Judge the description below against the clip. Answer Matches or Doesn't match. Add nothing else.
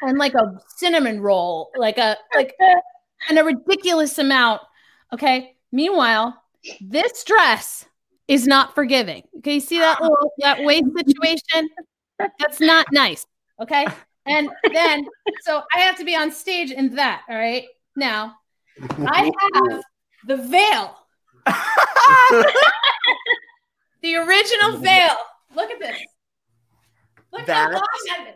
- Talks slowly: Matches